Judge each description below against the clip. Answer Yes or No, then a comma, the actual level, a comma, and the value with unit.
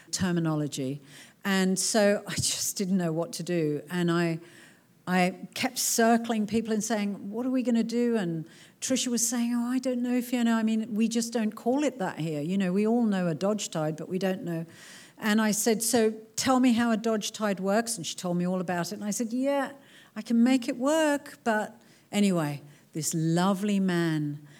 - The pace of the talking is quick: Yes, fast, 210 wpm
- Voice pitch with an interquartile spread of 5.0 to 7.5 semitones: Yes, wide, 5.4 semitones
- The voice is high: Yes, high, 205 Hz